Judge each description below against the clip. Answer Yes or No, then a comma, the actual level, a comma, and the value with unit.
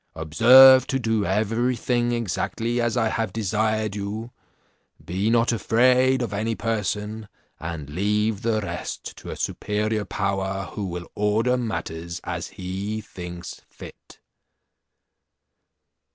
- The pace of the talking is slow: Yes, slow, 120 wpm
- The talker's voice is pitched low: Yes, low, 110 Hz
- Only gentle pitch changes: No, average, 3.1 semitones